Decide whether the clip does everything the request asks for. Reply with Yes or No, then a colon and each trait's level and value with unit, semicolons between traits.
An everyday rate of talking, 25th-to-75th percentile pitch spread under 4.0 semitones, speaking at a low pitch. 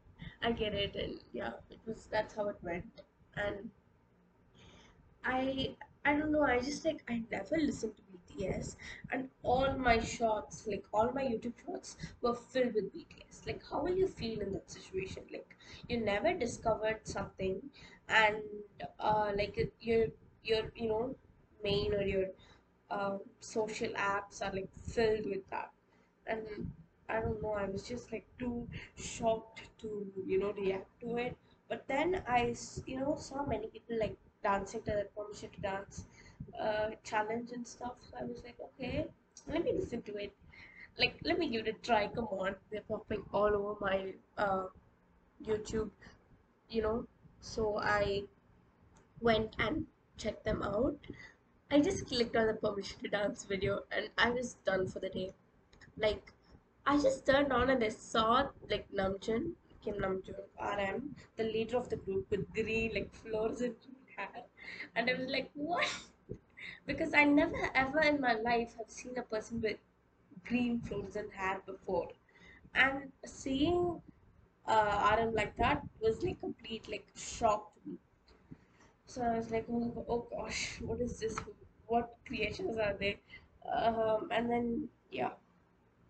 No: average, 160 wpm; average, 3.0 semitones; high, 220 Hz